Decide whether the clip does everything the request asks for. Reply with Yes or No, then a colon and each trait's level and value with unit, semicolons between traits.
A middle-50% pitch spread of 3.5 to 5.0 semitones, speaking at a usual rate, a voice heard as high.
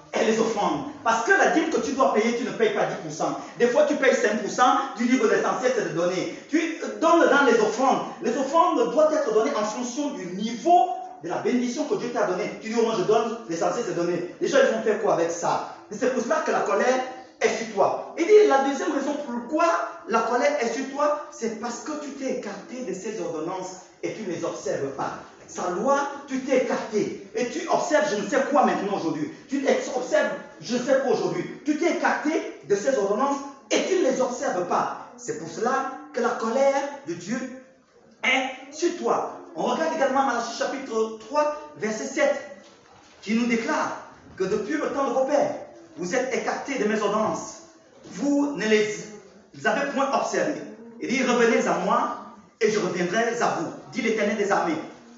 Yes: average, 4.5 semitones; average, 205 wpm; very high, 250 Hz